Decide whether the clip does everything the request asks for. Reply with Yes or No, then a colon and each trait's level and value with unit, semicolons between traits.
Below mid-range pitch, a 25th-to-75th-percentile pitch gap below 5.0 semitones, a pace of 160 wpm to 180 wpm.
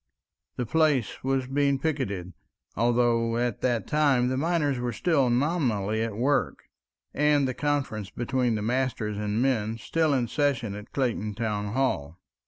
No: low, 125 Hz; average, 4.1 semitones; average, 145 wpm